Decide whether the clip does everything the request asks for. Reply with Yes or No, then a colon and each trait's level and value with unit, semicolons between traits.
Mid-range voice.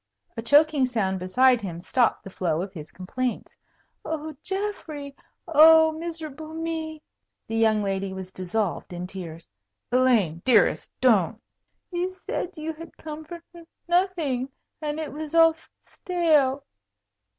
No: very high, 280 Hz